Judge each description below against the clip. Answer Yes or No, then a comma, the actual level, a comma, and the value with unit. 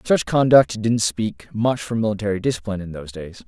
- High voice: No, low, 105 Hz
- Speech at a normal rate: Yes, average, 190 wpm